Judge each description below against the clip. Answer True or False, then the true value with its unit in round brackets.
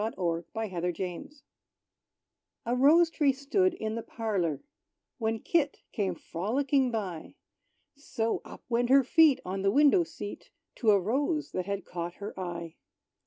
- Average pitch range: False (7.0 semitones)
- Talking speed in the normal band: True (150 wpm)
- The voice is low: False (225 Hz)